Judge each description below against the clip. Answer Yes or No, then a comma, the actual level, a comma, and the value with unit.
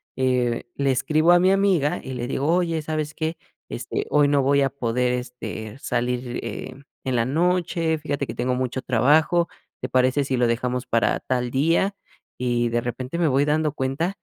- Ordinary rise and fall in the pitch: Yes, average, 4.0 semitones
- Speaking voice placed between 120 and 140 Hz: Yes, low, 135 Hz